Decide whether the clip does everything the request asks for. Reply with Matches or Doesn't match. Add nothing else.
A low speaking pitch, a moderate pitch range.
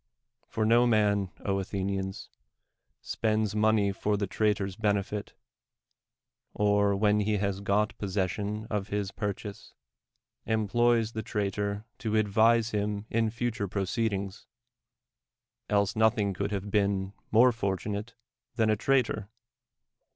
Doesn't match